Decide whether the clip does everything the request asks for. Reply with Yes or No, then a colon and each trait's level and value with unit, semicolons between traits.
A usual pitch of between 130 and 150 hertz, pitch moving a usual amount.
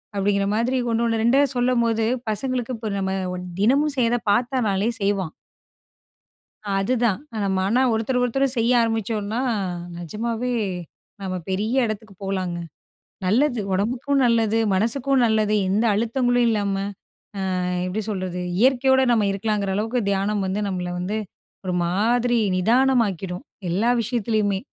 No: high, 220 Hz; average, 3.7 semitones